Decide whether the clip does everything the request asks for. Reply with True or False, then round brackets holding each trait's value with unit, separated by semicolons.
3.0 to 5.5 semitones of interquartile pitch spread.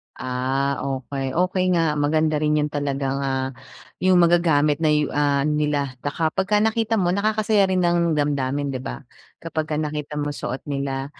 True (3.5 semitones)